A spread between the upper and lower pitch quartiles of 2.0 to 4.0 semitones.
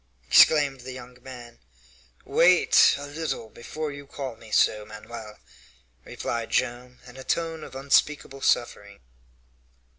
Yes: average, 3.4 semitones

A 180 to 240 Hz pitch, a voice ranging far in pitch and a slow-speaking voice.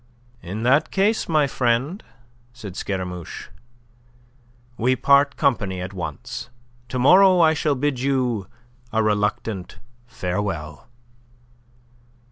No: low, 120 Hz; wide, 6.6 semitones; slow, 100 wpm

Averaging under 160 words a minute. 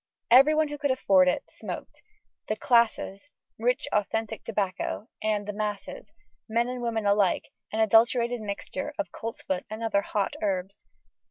Yes: average, 145 wpm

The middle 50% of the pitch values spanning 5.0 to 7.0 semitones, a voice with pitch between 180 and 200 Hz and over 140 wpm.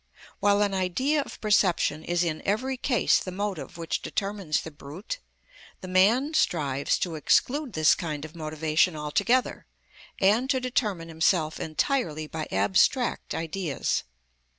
No: wide, 5.6 semitones; medium, 185 Hz; slow, 135 wpm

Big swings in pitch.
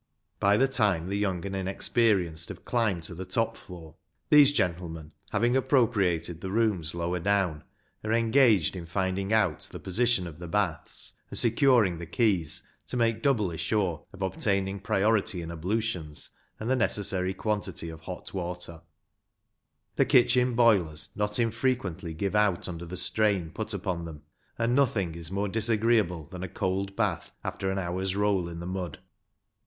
No: average, 4.2 semitones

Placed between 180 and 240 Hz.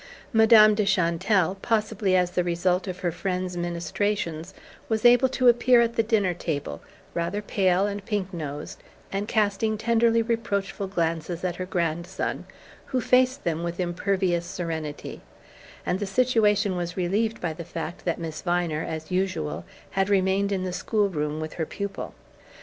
Yes: medium, 185 Hz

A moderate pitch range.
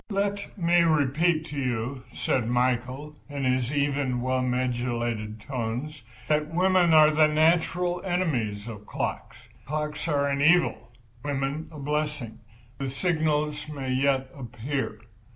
Yes: average, 3.7 semitones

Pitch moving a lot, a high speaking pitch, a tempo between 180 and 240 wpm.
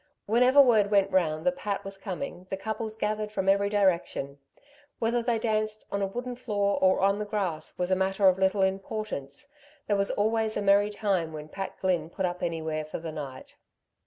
No: average, 2.9 semitones; high, 195 Hz; average, 195 wpm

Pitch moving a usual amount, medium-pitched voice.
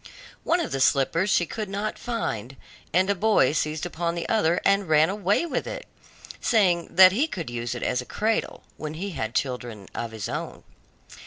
No: wide, 7.3 semitones; medium, 170 Hz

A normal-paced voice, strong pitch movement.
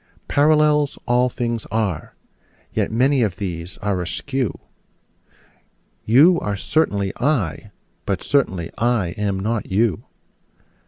No: slow, 110 wpm; wide, 5.7 semitones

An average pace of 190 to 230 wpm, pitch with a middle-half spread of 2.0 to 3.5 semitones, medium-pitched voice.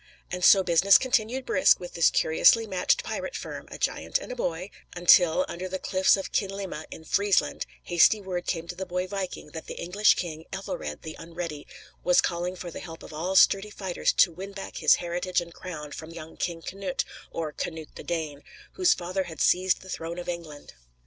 Yes: average, 200 wpm; average, 2.7 semitones; medium, 180 Hz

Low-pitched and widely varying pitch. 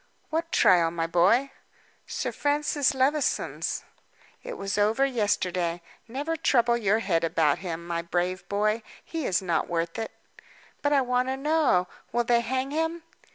No: high, 225 Hz; wide, 7.7 semitones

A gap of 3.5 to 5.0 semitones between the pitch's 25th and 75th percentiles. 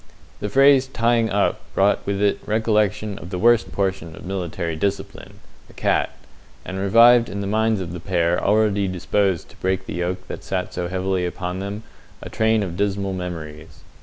No: average, 3.0 semitones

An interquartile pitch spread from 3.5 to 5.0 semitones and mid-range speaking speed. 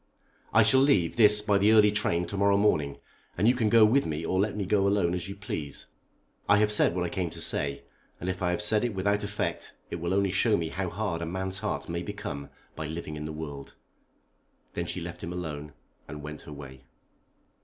No: average, 4.0 semitones; fast, 230 wpm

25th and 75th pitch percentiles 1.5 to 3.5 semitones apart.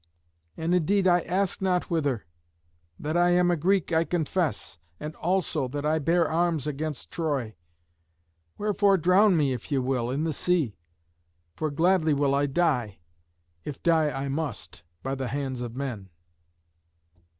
No: average, 4.4 semitones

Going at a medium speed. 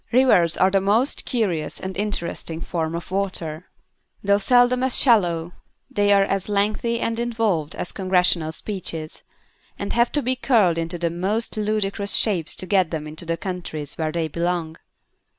Yes: average, 165 wpm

